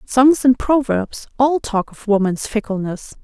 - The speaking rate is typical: Yes, average, 150 wpm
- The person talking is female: Yes, female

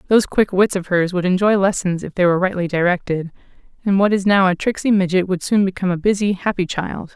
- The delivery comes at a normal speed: No, fast, 225 wpm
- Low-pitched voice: No, high, 190 Hz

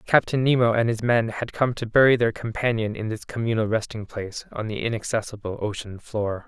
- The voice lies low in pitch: Yes, low, 115 Hz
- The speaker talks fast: No, average, 195 wpm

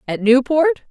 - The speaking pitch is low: No, very high, 265 Hz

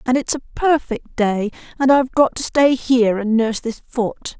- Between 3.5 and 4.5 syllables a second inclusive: No, 5.0 syllables/s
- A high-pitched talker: Yes, high, 245 Hz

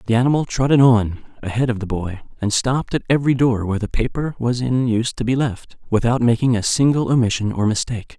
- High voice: No, low, 120 Hz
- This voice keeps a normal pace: No, fast, 220 wpm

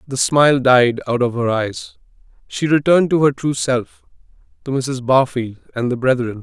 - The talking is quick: No, average, 175 wpm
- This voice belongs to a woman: No, male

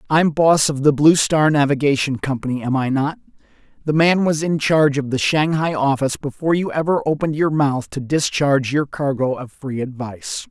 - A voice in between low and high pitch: Yes, medium, 145 Hz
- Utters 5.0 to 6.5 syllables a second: Yes, 5.4 syllables/s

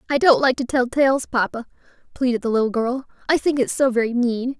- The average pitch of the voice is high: Yes, very high, 250 Hz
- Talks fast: Yes, fast, 220 wpm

